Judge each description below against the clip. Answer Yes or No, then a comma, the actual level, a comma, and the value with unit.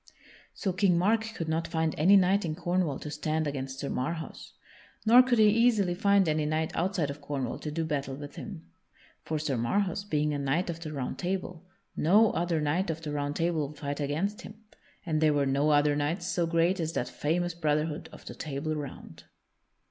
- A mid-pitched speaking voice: Yes, medium, 160 Hz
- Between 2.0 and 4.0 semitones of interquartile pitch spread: Yes, average, 3.6 semitones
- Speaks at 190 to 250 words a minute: Yes, average, 200 wpm